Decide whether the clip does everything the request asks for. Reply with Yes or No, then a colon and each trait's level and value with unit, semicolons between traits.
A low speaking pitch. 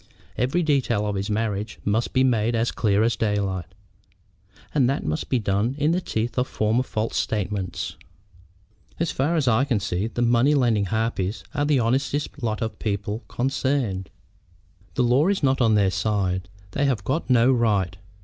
Yes: low, 115 Hz